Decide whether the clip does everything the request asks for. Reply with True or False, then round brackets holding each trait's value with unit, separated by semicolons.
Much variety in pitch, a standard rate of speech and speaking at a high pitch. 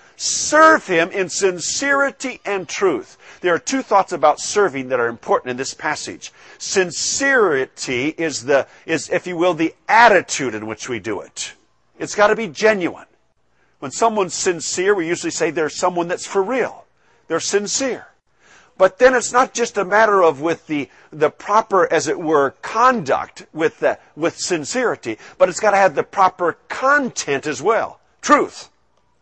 True (7.8 semitones; 165 wpm; 200 Hz)